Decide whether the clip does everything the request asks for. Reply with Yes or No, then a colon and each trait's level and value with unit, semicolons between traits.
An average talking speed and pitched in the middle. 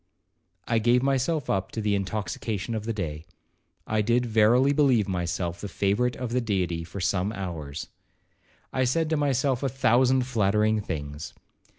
No: average, 155 wpm; low, 110 Hz